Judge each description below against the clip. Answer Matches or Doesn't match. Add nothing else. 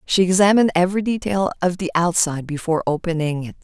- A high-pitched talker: Doesn't match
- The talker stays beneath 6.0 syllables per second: Doesn't match